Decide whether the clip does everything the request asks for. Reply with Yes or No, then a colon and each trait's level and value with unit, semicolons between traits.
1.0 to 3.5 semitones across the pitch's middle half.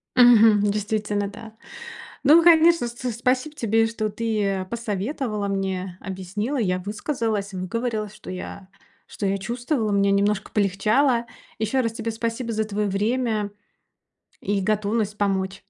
Yes: average, 2.8 semitones